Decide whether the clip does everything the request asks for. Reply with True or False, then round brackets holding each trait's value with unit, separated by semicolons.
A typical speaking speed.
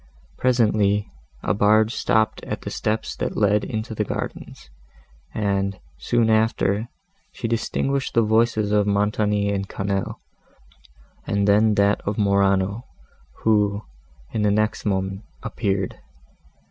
False (120 wpm)